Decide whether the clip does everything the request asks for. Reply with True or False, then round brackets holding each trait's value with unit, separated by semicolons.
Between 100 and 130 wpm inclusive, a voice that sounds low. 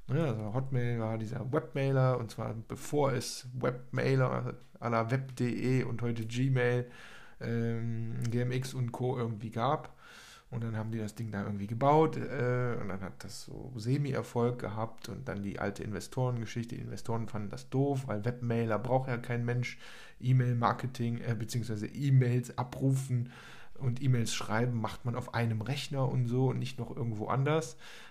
False (160 wpm; 120 Hz)